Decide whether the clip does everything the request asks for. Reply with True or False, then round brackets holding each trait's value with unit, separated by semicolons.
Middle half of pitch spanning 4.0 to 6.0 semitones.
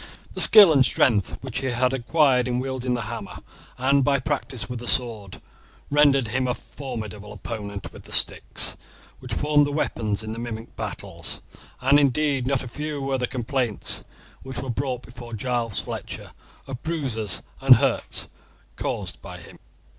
False (2.9 semitones)